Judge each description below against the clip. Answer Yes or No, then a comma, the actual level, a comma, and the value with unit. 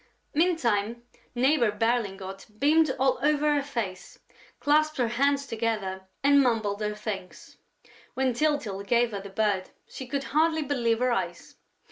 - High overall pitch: Yes, high, 240 Hz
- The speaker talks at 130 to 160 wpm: Yes, average, 140 wpm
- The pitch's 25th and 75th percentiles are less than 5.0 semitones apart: No, wide, 5.4 semitones